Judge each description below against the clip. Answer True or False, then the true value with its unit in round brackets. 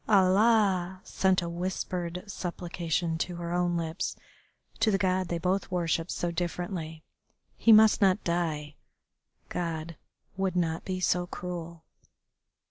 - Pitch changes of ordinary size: False (1.8 semitones)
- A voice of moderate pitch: True (175 Hz)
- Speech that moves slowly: True (130 wpm)